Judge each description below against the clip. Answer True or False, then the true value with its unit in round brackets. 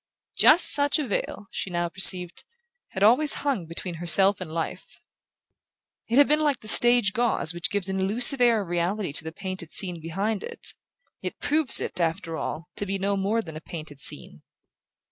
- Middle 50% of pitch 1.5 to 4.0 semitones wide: False (5.1 semitones)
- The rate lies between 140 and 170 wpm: False (185 wpm)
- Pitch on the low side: False (195 Hz)